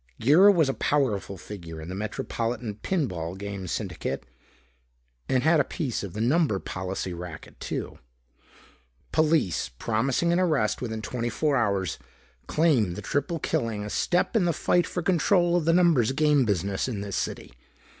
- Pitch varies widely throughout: Yes, wide, 8.0 semitones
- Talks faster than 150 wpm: Yes, average, 165 wpm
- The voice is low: Yes, low, 120 Hz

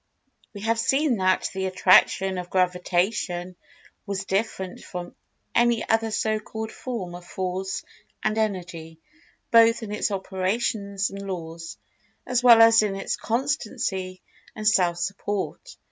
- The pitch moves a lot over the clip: No, average, 3.4 semitones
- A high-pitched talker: Yes, high, 200 Hz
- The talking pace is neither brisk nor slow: No, slow, 130 wpm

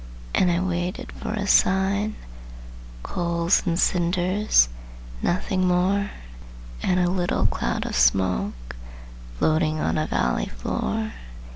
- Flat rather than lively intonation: No, average, 3.4 semitones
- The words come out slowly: Yes, slow, 115 wpm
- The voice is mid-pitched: Yes, medium, 180 Hz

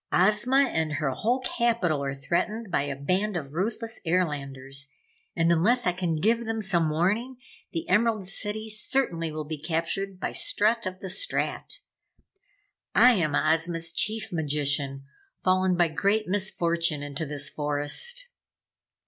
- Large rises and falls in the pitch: Yes, wide, 5.7 semitones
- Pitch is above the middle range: No, medium, 175 Hz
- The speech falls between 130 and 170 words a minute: Yes, average, 140 wpm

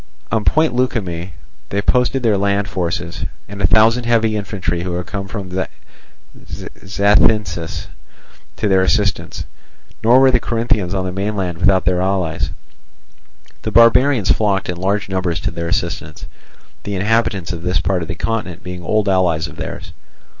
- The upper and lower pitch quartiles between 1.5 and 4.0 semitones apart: Yes, average, 3.4 semitones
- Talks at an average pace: Yes, average, 155 wpm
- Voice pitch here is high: No, very low, 95 Hz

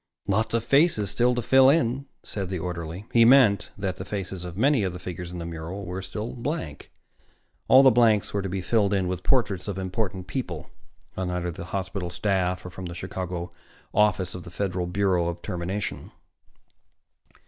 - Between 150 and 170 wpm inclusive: No, average, 180 wpm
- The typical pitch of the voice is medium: No, very low, 95 Hz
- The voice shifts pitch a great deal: No, average, 3.5 semitones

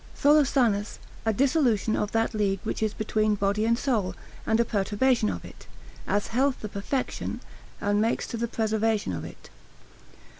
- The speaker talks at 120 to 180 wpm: Yes, average, 160 wpm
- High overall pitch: Yes, high, 220 Hz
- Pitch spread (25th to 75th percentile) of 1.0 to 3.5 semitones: Yes, narrow, 2.4 semitones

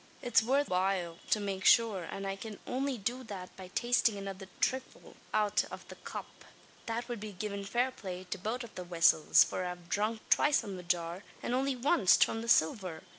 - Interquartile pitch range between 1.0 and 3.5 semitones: No, average, 4.5 semitones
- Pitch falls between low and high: No, high, 205 Hz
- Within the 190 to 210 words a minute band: Yes, average, 200 wpm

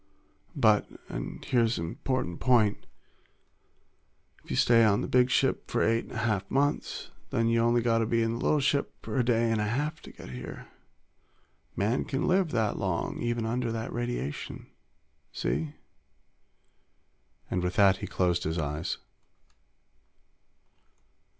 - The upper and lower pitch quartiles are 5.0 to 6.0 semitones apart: No, average, 3.8 semitones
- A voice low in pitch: Yes, low, 115 Hz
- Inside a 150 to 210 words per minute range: Yes, average, 155 wpm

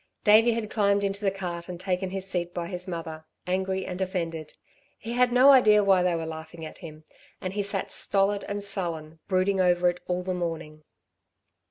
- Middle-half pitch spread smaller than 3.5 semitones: Yes, average, 2.8 semitones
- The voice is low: No, medium, 185 Hz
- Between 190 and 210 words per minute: Yes, average, 195 wpm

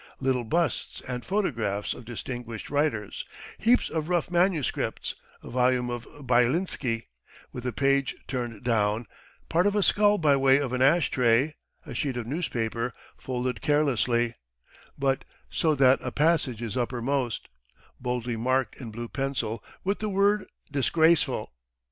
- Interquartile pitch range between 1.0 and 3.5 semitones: No, average, 4.4 semitones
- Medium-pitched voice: No, low, 130 Hz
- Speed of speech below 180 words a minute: Yes, average, 140 wpm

